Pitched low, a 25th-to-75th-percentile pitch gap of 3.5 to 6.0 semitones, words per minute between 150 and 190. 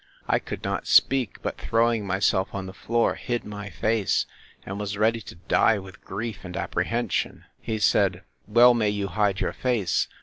No: low, 105 Hz; average, 3.0 semitones; average, 170 wpm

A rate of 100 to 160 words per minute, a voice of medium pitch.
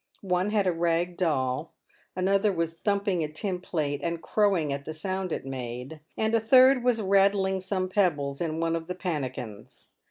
No: average, 180 wpm; medium, 180 Hz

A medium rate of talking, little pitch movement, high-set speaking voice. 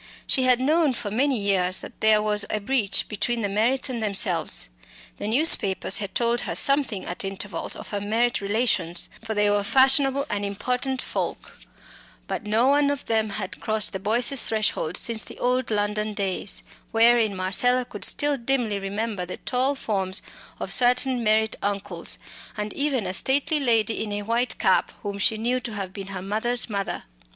No: average, 180 wpm; average, 3.7 semitones; high, 220 Hz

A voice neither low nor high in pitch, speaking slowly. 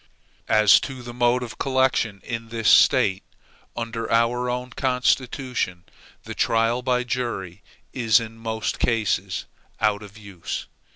No: low, 115 Hz; slow, 130 wpm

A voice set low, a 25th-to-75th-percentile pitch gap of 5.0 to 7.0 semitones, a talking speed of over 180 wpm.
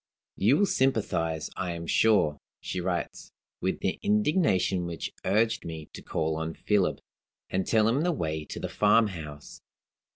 No: very low, 95 Hz; wide, 5.6 semitones; average, 155 wpm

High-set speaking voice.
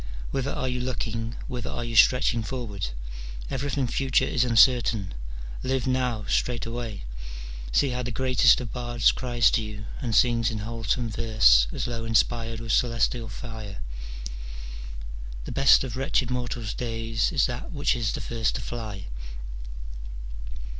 No: low, 115 Hz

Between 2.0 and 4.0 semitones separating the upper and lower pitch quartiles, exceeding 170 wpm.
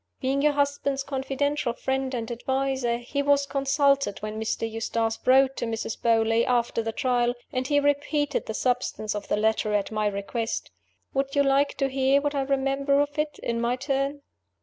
Yes: average, 3.3 semitones; average, 180 wpm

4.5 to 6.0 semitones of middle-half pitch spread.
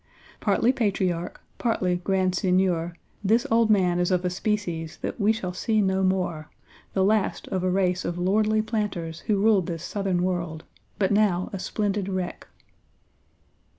No: average, 2.8 semitones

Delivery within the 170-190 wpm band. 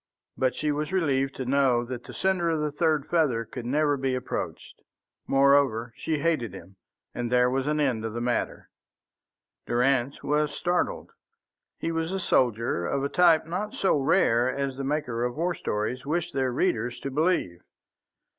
Yes: average, 175 wpm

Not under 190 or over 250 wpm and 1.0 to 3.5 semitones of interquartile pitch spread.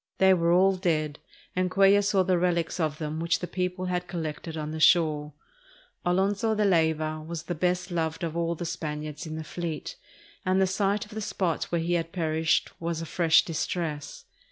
Yes: average, 195 wpm; narrow, 2.6 semitones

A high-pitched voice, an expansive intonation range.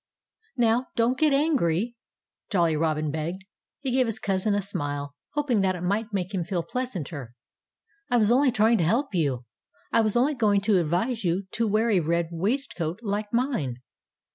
Yes: high, 200 Hz; wide, 5.8 semitones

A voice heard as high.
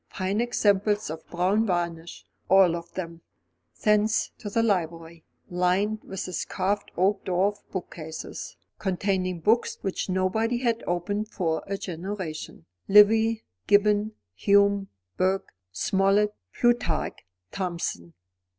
Yes: high, 195 Hz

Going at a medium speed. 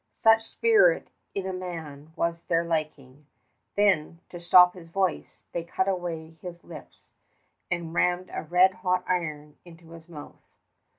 Yes: average, 155 wpm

